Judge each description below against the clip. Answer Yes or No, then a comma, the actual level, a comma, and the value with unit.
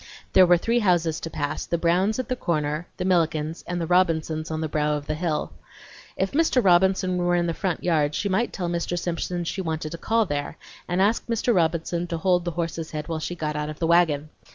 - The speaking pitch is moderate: Yes, medium, 170 Hz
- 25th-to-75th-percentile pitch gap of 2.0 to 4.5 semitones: Yes, narrow, 2.6 semitones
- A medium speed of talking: No, fast, 230 wpm